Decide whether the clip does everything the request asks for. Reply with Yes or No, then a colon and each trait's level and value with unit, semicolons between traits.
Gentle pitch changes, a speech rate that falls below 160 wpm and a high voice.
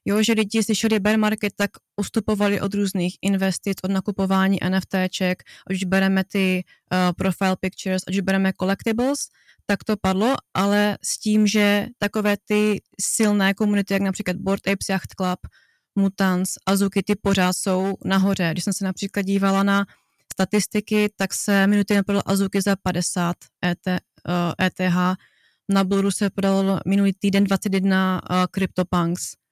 Yes: narrow, 1.4 semitones; average, 145 wpm; high, 195 Hz